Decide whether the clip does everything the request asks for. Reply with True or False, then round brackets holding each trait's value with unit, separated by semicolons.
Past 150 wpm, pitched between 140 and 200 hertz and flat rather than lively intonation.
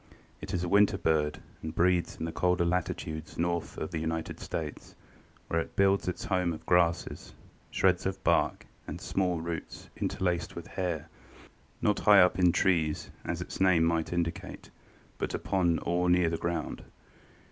False (165 wpm; 85 Hz; 1.9 semitones)